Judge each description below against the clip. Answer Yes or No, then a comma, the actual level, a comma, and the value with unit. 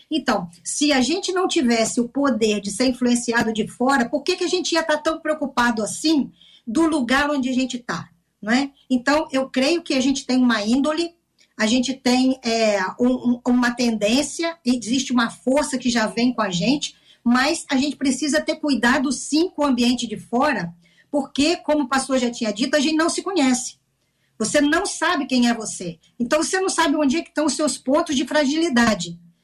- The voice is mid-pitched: No, very high, 265 Hz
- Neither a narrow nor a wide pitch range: Yes, average, 4.2 semitones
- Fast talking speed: Yes, fast, 200 wpm